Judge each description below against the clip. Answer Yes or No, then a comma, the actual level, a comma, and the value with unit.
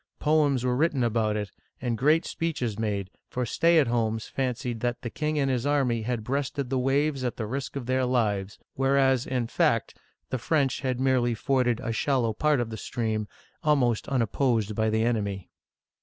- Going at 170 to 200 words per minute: Yes, average, 185 wpm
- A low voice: Yes, low, 125 Hz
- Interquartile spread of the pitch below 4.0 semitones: Yes, average, 3.4 semitones